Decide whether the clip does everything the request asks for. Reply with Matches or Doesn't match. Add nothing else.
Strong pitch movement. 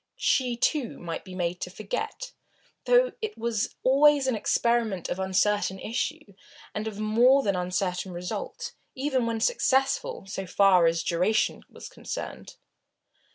Matches